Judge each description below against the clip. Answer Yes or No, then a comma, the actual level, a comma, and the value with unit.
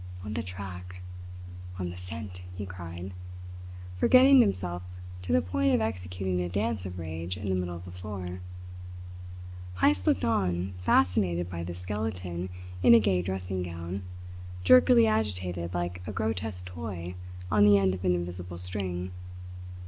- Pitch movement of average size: No, narrow, 1.7 semitones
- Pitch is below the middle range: Yes, very low, 90 Hz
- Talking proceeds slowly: No, average, 150 wpm